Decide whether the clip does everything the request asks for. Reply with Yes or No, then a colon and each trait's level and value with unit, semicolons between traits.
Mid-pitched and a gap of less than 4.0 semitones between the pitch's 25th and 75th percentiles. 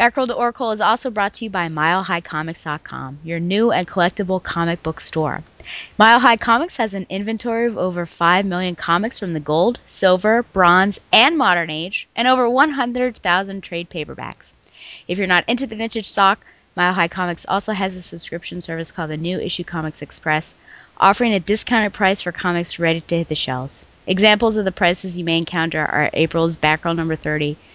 No: medium, 180 Hz; average, 4.5 semitones